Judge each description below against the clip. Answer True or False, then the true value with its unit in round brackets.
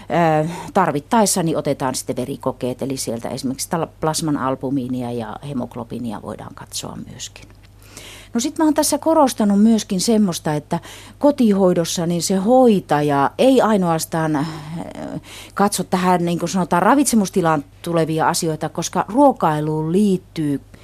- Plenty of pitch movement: True (6.2 semitones)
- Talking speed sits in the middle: True (120 wpm)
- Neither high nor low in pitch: True (165 Hz)